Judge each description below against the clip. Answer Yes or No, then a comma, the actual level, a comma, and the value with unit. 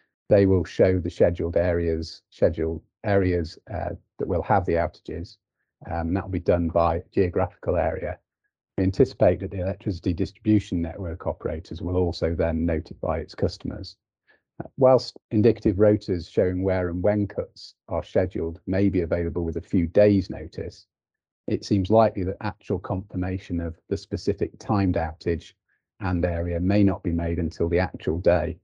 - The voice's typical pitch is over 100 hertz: No, very low, 90 Hz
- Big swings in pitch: No, average, 2.9 semitones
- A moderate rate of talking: Yes, average, 160 wpm